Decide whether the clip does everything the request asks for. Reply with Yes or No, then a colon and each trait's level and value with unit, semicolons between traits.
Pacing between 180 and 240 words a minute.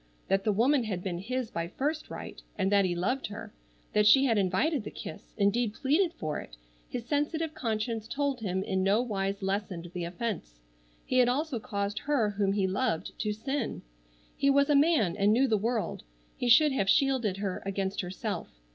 Yes: average, 190 wpm